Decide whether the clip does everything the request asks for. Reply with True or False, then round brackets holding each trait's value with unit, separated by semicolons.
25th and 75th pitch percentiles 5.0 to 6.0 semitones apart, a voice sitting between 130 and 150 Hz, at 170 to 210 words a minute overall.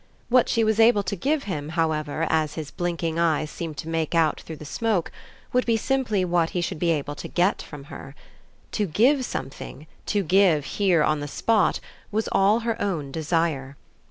False (5.3 semitones; 170 Hz; 190 wpm)